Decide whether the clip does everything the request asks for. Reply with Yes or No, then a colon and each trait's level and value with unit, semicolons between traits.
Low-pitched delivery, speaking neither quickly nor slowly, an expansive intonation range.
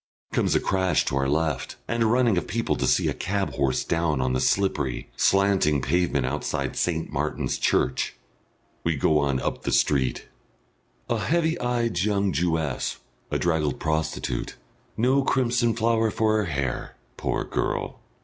Yes: very low, 85 Hz; average, 160 wpm; wide, 7.2 semitones